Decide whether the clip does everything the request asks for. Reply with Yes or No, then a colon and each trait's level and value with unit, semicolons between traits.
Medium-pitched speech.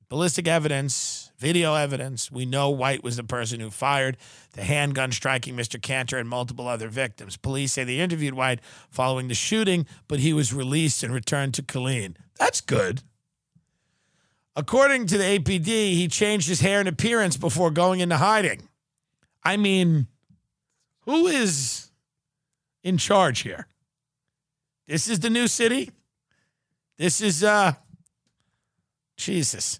Yes: medium, 145 Hz